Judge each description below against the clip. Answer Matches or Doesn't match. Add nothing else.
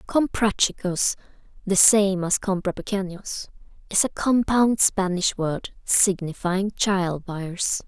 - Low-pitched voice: Doesn't match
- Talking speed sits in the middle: Doesn't match